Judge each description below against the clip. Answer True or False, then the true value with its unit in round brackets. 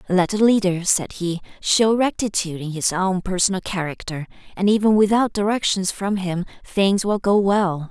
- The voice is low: False (190 Hz)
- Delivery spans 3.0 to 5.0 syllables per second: True (4.9 syllables/s)